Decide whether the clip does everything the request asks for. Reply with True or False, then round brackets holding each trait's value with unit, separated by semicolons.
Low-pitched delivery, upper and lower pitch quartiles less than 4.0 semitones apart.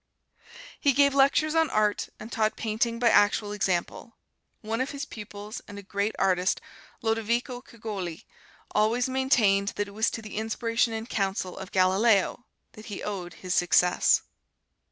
False (215 Hz; 2.9 semitones)